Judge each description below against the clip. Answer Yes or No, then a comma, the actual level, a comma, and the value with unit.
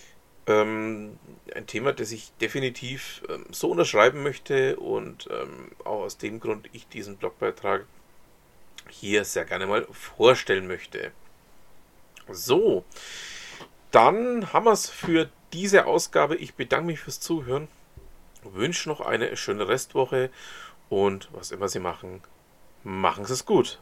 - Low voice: No, medium, 165 Hz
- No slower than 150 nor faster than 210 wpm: No, slow, 125 wpm